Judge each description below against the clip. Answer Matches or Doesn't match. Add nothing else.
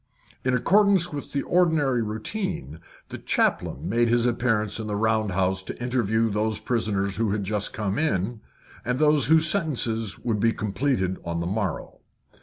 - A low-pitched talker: Matches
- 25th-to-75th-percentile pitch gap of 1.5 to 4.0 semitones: Doesn't match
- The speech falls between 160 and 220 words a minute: Matches